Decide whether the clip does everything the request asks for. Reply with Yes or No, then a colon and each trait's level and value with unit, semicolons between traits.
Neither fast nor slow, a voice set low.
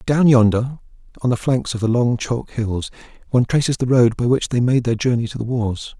No: fast, 230 wpm; low, 120 Hz